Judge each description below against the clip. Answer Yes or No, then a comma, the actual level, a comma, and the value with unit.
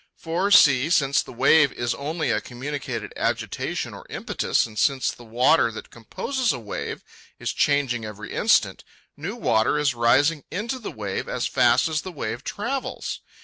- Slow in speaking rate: No, average, 165 wpm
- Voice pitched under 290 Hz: Yes, medium, 140 Hz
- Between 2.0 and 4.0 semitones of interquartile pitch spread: No, wide, 5.5 semitones